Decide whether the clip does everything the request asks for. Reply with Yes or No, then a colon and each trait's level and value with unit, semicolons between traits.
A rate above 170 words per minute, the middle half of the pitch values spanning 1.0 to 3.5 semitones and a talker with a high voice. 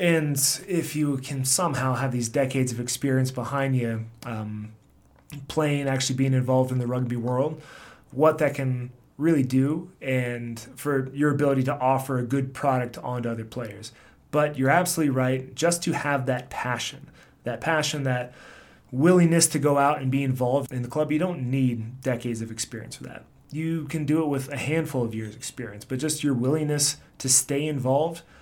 No: average, 180 wpm; average, 3.0 semitones; low, 135 Hz